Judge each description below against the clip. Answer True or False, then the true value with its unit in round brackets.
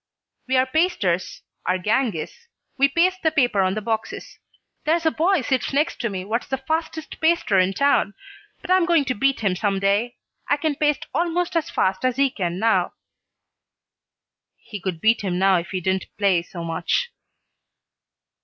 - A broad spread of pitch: True (8.3 semitones)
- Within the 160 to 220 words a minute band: True (180 wpm)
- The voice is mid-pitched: False (240 Hz)